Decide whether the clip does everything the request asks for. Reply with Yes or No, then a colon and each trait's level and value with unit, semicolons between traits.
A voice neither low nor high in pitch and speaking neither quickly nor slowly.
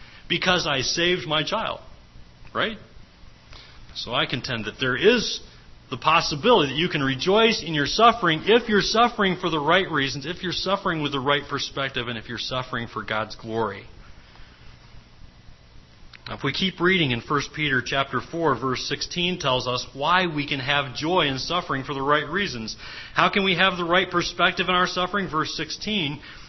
Yes: medium, 150 Hz; average, 180 wpm